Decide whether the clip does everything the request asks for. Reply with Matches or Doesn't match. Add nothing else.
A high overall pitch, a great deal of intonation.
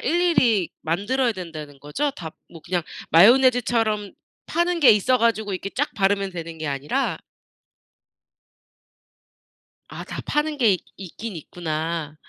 Matches